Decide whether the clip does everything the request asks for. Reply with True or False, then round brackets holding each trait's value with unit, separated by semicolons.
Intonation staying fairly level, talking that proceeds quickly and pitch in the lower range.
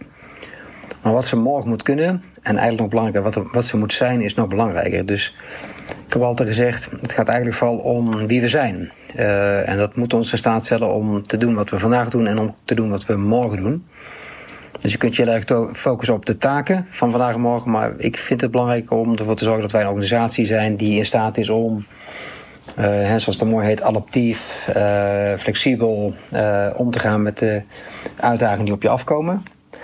True (2.3 semitones; 220 wpm; 115 Hz)